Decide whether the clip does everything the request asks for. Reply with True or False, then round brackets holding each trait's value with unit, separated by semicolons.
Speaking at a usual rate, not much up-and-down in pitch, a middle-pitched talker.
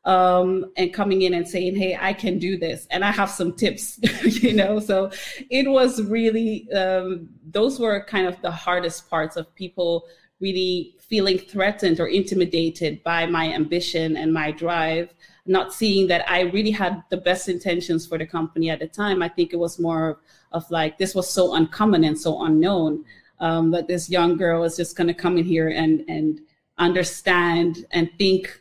True (190 wpm; 2.3 semitones; 180 Hz)